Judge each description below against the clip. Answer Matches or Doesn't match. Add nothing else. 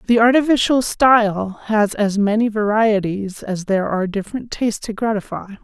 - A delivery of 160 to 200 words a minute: Doesn't match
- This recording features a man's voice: Doesn't match